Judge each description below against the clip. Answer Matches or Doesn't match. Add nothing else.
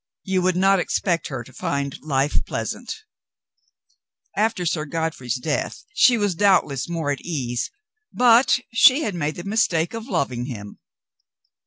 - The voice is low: Doesn't match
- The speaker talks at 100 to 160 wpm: Matches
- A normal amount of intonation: Doesn't match